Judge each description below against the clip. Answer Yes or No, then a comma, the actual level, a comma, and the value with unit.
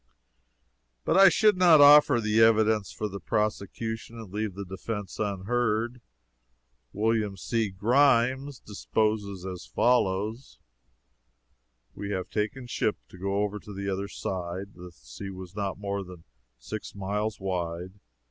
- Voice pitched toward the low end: Yes, low, 105 Hz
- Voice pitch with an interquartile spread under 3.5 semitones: Yes, average, 2.8 semitones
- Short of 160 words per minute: Yes, slow, 135 wpm